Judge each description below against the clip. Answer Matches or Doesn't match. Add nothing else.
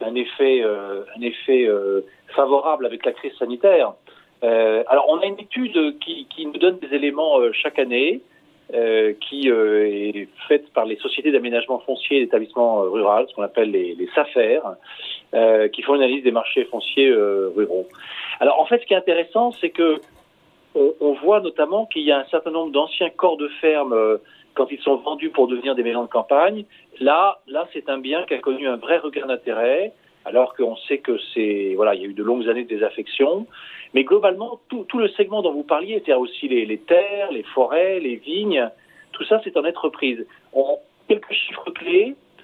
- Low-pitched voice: Doesn't match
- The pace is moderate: Matches